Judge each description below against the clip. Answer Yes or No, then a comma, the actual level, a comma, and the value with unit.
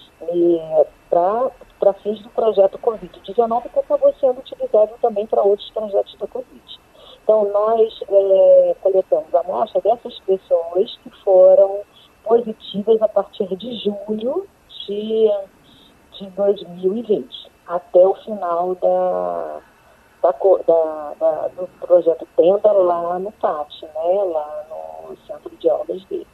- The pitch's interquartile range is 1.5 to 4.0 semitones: No, average, 5.1 semitones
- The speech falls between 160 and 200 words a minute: No, slow, 120 wpm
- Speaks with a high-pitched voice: Yes, high, 205 Hz